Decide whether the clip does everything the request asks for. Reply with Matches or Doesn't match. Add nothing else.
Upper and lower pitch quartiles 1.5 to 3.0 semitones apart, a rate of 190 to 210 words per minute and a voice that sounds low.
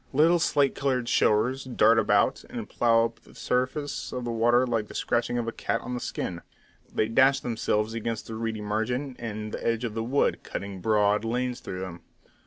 Matches